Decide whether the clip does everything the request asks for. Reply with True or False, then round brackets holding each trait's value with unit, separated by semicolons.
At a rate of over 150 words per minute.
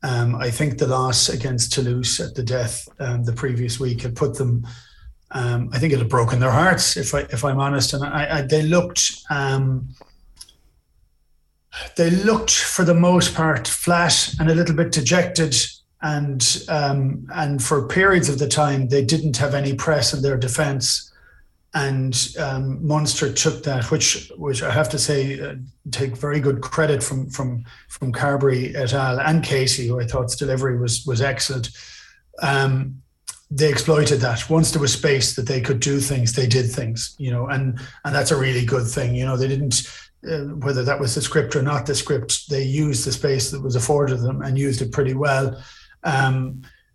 True (190 wpm)